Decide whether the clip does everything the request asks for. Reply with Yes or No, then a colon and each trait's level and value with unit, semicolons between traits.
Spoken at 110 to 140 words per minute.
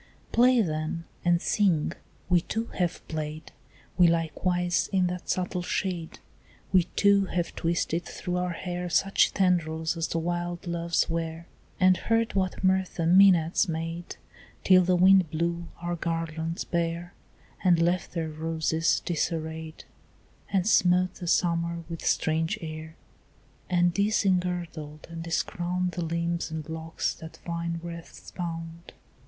Yes: slow, 135 wpm